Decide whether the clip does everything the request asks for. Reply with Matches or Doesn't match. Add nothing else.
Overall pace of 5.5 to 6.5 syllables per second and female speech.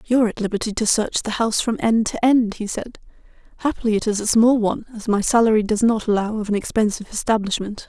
Matches